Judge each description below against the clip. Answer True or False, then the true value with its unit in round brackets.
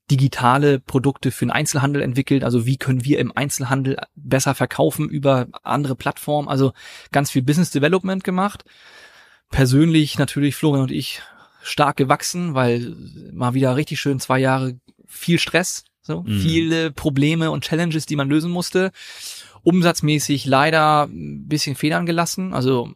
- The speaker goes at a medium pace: True (145 wpm)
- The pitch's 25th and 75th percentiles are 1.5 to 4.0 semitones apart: True (2.9 semitones)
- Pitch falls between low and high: True (145 Hz)